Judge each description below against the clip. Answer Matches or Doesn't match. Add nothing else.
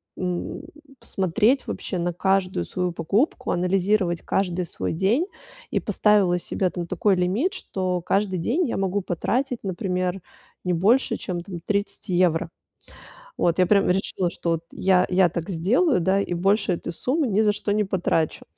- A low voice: Doesn't match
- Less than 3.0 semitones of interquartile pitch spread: Matches